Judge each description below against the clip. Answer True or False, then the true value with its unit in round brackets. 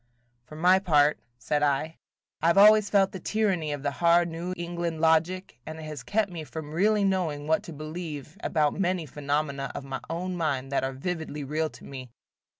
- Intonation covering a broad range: False (3.5 semitones)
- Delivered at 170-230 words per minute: True (195 wpm)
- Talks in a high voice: False (160 Hz)